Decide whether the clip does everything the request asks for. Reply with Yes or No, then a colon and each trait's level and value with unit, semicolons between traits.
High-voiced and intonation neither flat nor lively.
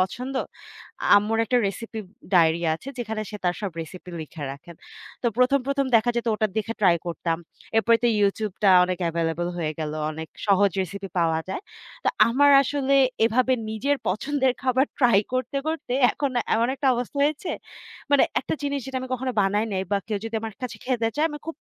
No: high, 225 Hz; wide, 5.9 semitones